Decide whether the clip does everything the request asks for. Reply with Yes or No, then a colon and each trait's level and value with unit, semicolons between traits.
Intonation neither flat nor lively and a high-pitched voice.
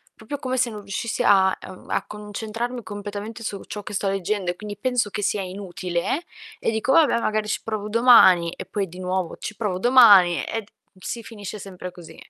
Yes: average, 3.1 semitones; high, 205 Hz